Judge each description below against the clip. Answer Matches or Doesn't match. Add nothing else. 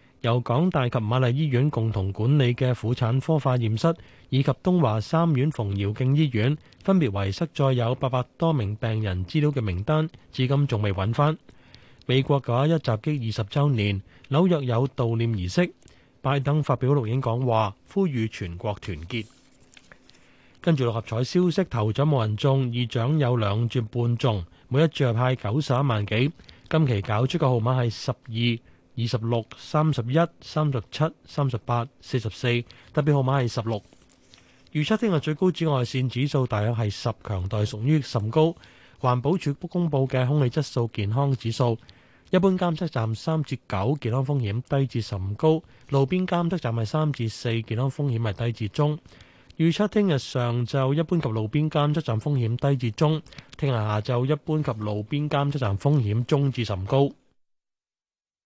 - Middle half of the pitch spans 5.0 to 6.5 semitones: Doesn't match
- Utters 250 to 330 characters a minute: Matches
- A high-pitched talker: Doesn't match